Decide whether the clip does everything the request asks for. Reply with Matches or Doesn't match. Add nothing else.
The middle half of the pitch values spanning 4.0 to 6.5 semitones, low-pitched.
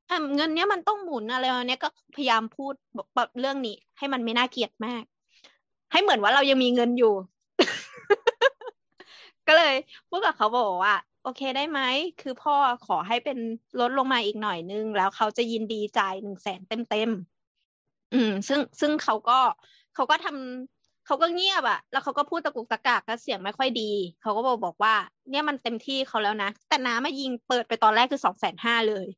Doesn't match